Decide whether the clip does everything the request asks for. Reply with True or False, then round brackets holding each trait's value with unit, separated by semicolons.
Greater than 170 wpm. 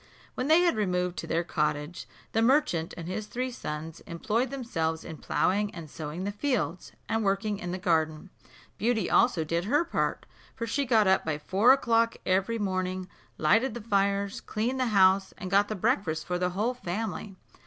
True (185 wpm)